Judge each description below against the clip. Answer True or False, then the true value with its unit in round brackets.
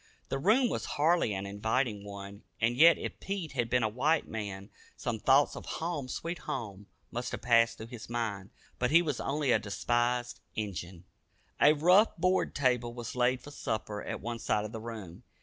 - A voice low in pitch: True (120 Hz)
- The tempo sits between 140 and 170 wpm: False (190 wpm)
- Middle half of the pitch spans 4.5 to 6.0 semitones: True (5.1 semitones)